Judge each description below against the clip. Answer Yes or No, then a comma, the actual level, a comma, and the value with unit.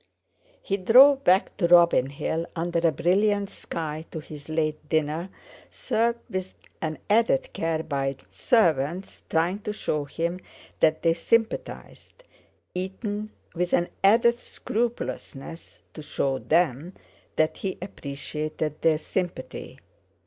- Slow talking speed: Yes, slow, 120 wpm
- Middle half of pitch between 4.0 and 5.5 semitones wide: Yes, average, 4.4 semitones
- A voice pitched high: No, medium, 170 Hz